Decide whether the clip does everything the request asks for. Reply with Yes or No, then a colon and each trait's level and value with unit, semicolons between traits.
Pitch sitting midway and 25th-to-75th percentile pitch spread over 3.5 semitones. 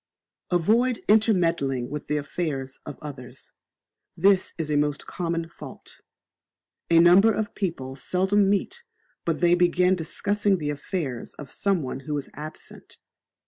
Yes: medium, 170 Hz; average, 4.7 semitones